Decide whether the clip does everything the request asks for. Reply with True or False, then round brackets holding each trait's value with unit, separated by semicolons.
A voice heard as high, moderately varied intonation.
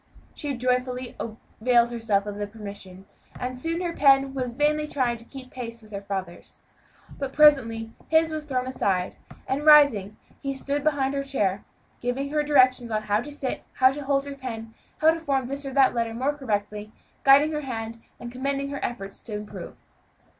True (255 Hz; 3.9 semitones)